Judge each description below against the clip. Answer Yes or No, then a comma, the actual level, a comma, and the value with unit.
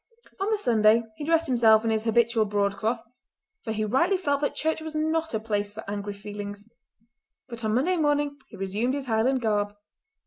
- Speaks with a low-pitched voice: No, high, 230 Hz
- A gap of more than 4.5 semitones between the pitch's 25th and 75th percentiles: Yes, wide, 5.6 semitones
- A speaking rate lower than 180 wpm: No, average, 185 wpm